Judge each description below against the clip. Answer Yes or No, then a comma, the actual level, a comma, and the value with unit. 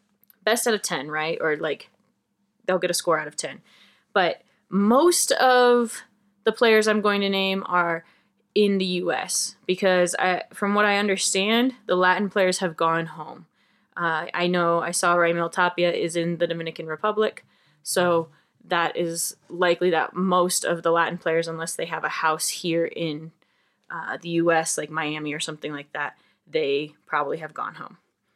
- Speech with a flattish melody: No, average, 3.7 semitones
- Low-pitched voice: No, medium, 180 Hz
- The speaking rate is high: No, average, 175 wpm